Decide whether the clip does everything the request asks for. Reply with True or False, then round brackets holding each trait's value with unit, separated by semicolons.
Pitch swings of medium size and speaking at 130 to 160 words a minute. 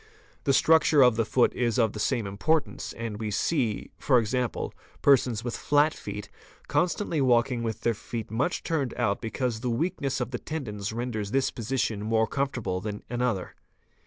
False (3.7 semitones; 180 wpm)